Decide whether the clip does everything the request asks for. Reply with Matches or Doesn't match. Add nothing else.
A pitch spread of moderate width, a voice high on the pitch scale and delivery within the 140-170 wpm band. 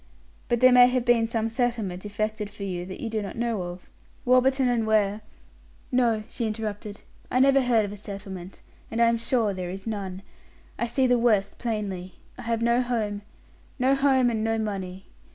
Doesn't match